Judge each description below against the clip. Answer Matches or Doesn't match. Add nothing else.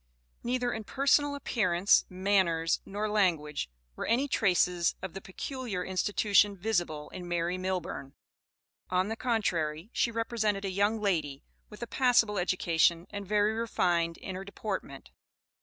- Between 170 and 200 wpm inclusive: Doesn't match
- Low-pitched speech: Doesn't match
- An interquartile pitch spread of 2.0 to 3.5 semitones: Doesn't match